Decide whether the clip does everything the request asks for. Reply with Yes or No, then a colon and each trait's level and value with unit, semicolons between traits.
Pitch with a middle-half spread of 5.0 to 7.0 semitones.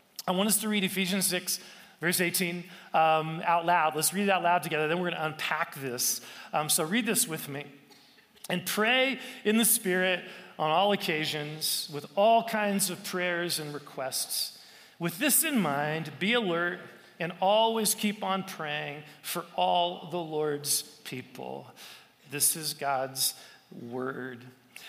No: average, 4.2 semitones